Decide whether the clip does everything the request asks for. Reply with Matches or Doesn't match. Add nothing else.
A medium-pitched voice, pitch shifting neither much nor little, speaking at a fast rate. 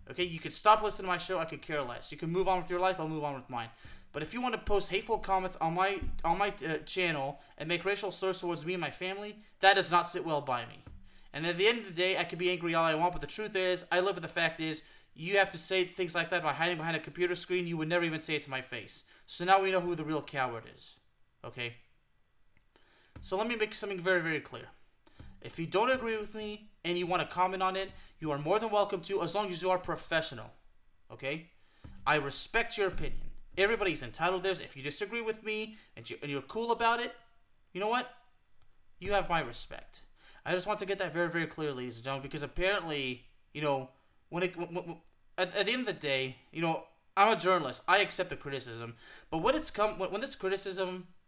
Matches